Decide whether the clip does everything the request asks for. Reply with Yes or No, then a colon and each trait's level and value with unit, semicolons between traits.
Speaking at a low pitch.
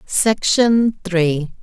No: high, 195 Hz